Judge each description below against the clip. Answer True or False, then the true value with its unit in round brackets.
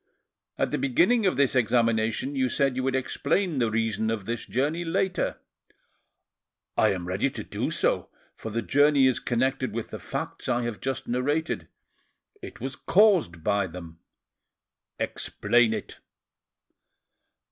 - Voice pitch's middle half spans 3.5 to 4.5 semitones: True (4.2 semitones)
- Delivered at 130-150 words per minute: True (145 wpm)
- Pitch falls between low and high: False (125 Hz)